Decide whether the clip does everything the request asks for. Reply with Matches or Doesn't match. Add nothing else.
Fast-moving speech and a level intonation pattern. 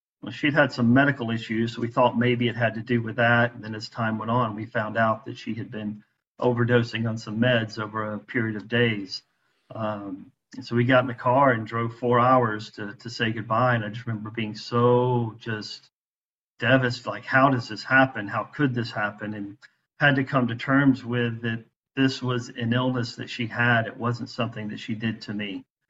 Matches